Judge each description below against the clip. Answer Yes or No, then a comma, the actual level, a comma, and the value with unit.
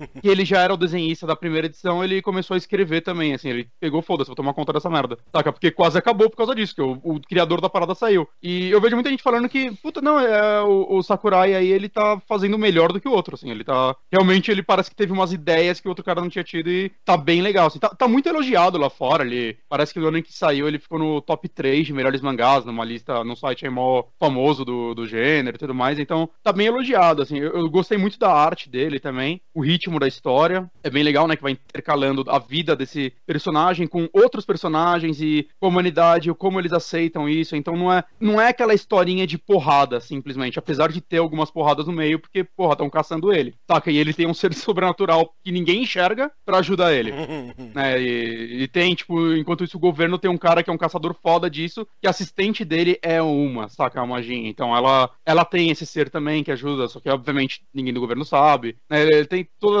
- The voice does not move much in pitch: No, average, 4.5 semitones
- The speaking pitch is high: No, medium, 165 Hz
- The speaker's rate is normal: No, fast, 235 wpm